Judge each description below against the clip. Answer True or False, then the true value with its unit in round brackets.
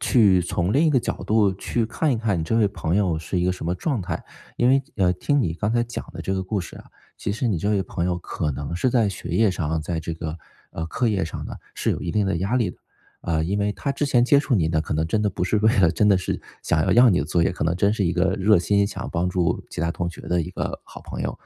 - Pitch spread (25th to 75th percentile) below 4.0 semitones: False (4.4 semitones)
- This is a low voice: True (95 Hz)